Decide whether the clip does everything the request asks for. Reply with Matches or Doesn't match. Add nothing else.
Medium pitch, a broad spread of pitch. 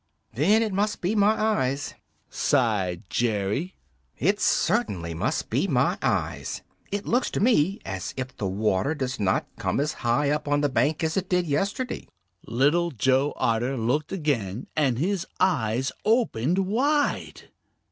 Matches